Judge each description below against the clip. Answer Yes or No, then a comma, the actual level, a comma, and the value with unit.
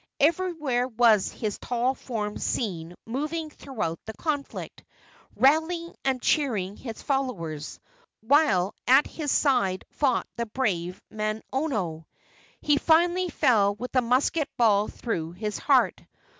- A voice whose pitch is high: Yes, high, 245 Hz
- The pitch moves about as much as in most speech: No, wide, 5.7 semitones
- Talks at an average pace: No, slow, 120 wpm